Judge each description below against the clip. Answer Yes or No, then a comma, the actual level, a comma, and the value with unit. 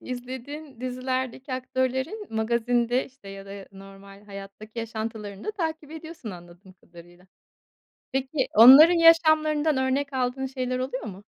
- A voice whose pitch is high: Yes, very high, 255 Hz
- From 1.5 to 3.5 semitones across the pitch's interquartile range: No, average, 4.9 semitones